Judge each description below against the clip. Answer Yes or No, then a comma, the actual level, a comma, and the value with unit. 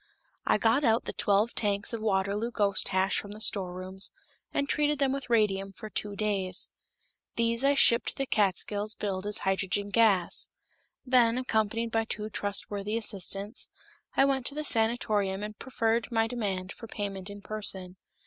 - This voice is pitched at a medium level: No, high, 210 Hz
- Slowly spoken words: No, average, 165 wpm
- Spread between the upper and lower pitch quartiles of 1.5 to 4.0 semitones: Yes, average, 2.8 semitones